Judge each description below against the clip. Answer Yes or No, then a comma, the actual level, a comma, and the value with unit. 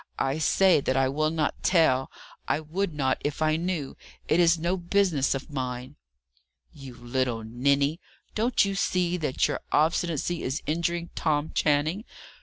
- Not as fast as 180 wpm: Yes, average, 155 wpm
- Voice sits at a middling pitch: Yes, medium, 155 Hz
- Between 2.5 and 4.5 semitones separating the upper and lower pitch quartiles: Yes, average, 4.2 semitones